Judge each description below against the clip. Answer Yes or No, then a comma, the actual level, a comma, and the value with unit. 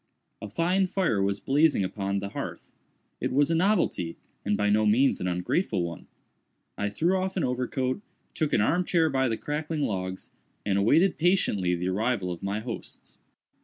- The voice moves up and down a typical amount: No, wide, 8.4 semitones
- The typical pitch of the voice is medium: No, low, 115 Hz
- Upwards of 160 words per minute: Yes, average, 175 wpm